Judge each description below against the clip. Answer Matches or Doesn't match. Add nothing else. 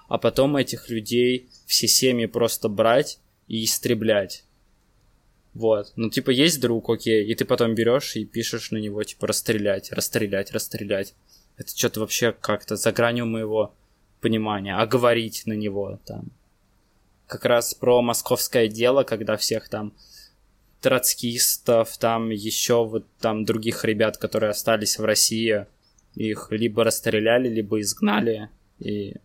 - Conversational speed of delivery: Matches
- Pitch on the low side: Matches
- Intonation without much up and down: Matches